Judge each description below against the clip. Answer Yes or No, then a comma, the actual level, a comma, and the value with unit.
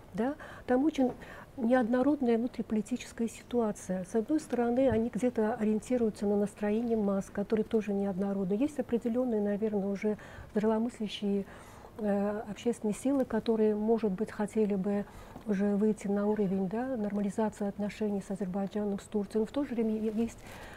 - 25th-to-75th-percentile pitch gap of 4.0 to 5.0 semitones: No, narrow, 2.5 semitones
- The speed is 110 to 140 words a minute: Yes, average, 135 wpm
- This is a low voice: No, high, 215 Hz